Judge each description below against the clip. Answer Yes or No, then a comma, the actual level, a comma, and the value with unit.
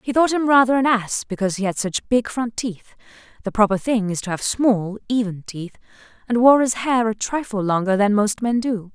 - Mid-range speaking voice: No, high, 220 Hz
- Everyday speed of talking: No, fast, 220 wpm